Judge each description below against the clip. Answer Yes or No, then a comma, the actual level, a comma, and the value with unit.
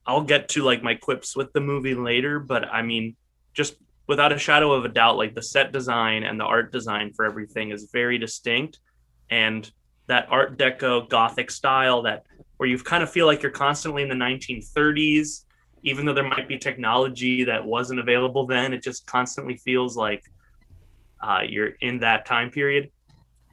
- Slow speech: No, average, 185 wpm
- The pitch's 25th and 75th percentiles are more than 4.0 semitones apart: No, average, 3.7 semitones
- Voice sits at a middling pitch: No, low, 125 Hz